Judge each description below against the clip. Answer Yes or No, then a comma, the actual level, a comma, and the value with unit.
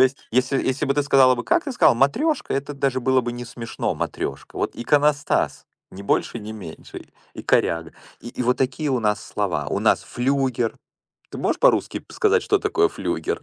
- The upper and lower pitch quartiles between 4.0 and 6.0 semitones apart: No, average, 3.3 semitones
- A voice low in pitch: Yes, low, 130 Hz